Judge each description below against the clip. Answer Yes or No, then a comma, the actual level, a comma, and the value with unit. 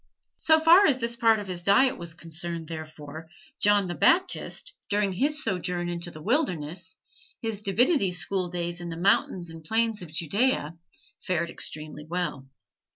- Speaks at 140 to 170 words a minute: Yes, average, 155 wpm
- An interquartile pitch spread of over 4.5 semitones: Yes, average, 5.1 semitones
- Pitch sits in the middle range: Yes, medium, 180 Hz